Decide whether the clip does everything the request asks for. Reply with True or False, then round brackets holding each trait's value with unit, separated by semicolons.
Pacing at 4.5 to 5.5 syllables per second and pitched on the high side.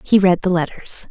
False (5.0 syllables/s; 180 Hz)